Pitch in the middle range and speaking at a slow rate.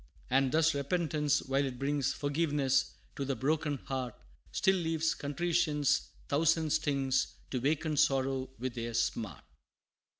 Yes: medium, 145 Hz; slow, 130 wpm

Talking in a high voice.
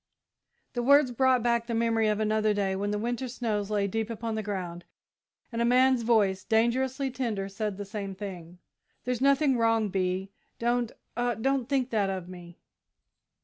Yes: high, 225 Hz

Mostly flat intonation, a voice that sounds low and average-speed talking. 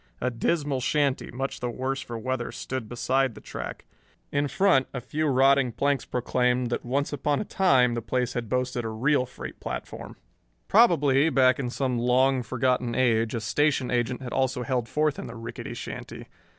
Yes: narrow, 2.1 semitones; low, 130 Hz; average, 180 wpm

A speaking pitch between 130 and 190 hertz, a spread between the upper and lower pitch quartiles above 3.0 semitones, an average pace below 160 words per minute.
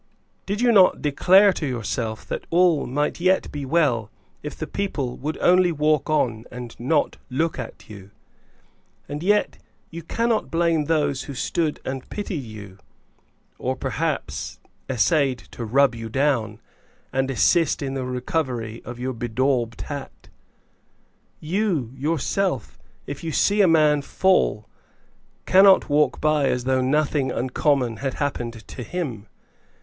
Yes: medium, 140 Hz; average, 4.8 semitones; average, 145 wpm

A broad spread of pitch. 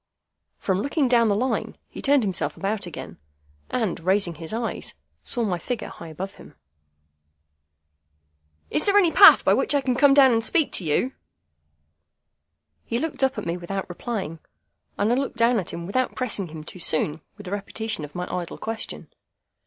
Yes: wide, 6.1 semitones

